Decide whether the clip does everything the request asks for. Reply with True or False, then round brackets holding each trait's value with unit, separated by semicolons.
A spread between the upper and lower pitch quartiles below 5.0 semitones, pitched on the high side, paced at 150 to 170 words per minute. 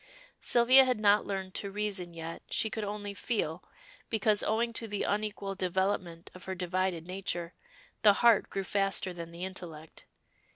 True (2.8 semitones; 195 Hz; 160 wpm)